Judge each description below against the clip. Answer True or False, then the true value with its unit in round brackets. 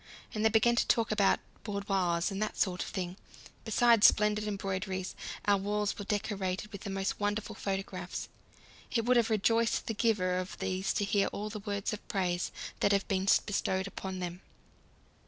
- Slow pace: False (175 wpm)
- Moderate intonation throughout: False (2.0 semitones)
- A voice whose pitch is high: True (200 Hz)